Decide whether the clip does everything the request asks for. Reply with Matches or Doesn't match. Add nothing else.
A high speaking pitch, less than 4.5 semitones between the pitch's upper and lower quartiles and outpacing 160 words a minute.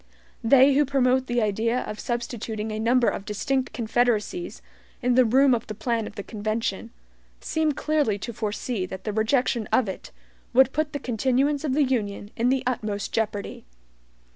Matches